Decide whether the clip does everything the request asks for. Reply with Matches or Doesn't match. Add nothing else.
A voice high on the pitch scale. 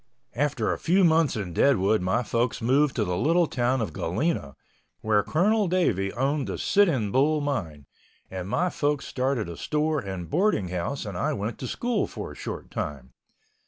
Doesn't match